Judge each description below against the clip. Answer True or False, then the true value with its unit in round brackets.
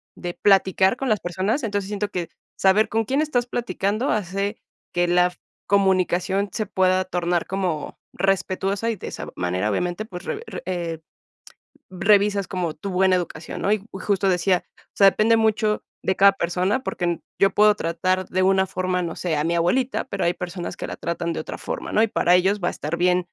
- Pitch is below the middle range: False (190 Hz)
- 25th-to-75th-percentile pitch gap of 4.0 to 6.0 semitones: False (2.6 semitones)